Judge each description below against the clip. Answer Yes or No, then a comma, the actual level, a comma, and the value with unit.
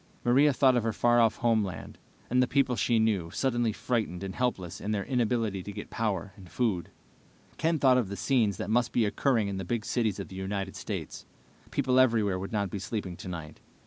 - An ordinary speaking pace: No, fast, 210 wpm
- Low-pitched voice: Yes, low, 110 Hz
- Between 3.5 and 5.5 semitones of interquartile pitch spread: Yes, average, 4.0 semitones